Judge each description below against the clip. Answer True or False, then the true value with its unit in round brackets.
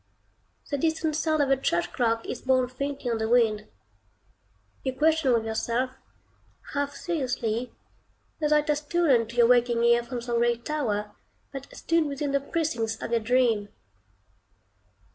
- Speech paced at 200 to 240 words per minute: False (155 wpm)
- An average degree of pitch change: True (3.9 semitones)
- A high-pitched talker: True (250 Hz)